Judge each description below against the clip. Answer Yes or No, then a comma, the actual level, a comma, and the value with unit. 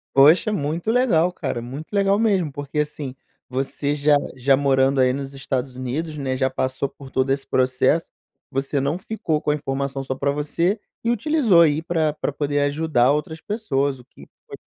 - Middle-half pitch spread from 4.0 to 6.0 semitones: No, average, 3.3 semitones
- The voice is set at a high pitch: No, medium, 145 Hz